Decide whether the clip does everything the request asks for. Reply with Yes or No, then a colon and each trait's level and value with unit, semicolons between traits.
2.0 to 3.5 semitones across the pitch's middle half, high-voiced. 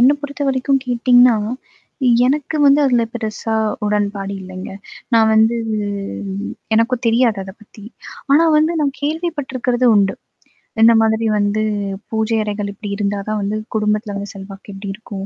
No: average, 3.9 semitones; high, 220 Hz